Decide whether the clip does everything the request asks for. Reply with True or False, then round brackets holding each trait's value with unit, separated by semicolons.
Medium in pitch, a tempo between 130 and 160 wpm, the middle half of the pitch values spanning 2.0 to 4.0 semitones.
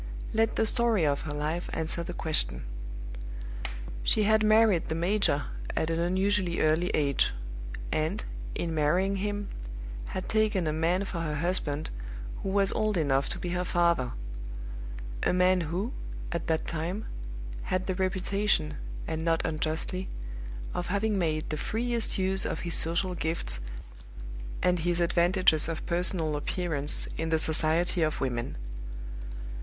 True (175 Hz; 145 wpm; 3.3 semitones)